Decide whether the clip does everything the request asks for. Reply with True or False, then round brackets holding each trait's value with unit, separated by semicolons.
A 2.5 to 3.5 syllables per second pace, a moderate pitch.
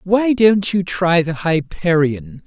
True (3.4 syllables/s; 175 Hz)